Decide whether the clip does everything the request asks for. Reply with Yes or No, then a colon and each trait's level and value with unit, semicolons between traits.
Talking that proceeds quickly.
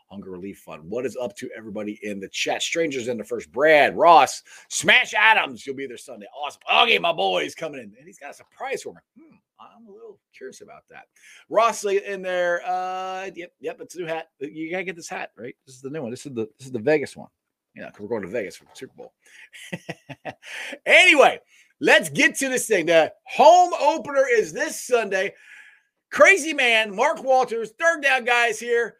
Yes: fast, 215 wpm